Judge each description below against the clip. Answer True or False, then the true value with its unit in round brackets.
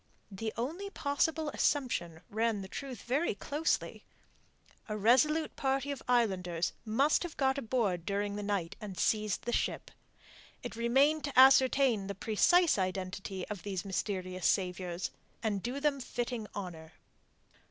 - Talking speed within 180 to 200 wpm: False (140 wpm)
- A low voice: False (220 Hz)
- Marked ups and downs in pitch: True (5.9 semitones)